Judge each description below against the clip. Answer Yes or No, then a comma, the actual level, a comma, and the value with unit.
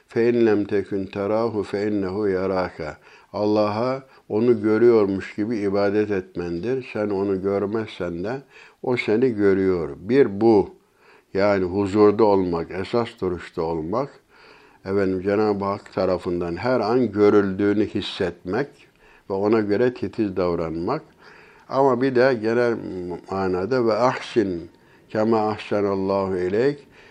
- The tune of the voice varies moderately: Yes, average, 3.0 semitones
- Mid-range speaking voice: No, low, 100 Hz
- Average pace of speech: Yes, average, 110 wpm